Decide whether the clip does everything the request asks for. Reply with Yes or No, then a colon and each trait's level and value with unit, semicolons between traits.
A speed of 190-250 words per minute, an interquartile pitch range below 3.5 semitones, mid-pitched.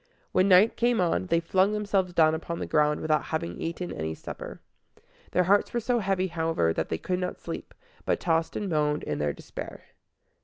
No: average, 195 wpm; average, 3.9 semitones; medium, 170 Hz